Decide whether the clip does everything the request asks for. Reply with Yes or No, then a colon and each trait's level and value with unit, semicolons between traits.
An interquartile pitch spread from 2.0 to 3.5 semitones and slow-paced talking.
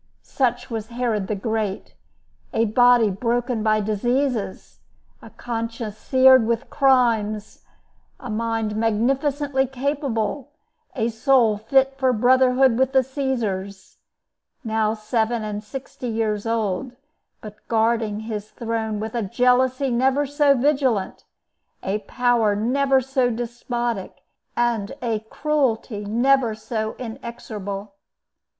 Yes: average, 3.1 semitones; slow, 110 wpm